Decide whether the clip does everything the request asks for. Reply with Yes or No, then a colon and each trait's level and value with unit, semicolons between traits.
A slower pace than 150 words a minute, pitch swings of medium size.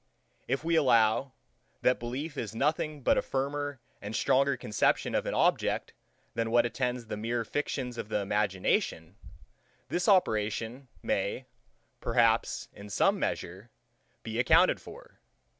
Yes: slow, 135 wpm; average, 4.2 semitones